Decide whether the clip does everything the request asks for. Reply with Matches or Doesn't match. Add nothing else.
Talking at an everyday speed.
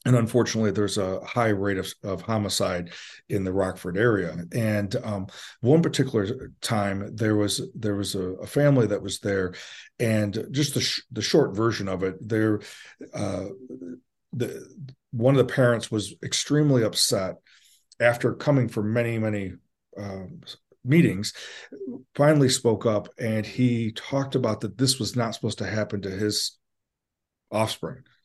Matches